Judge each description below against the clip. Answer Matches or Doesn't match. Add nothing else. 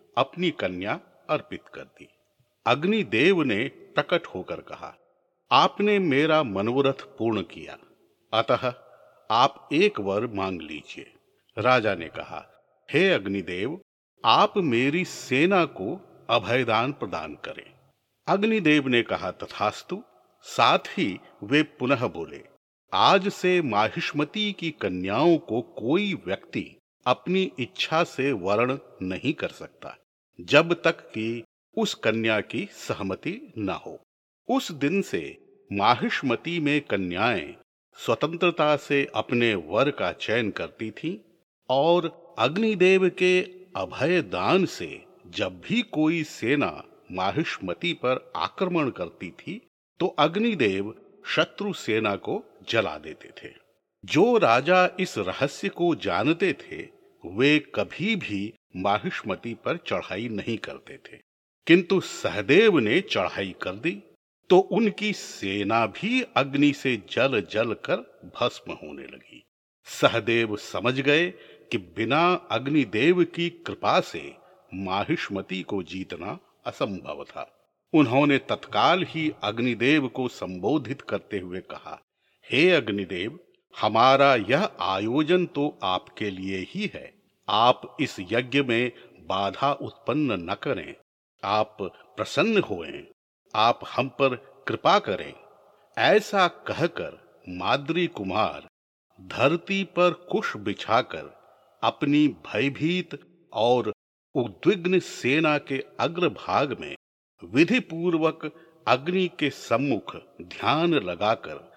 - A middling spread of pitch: Doesn't match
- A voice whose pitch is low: Doesn't match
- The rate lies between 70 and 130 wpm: Matches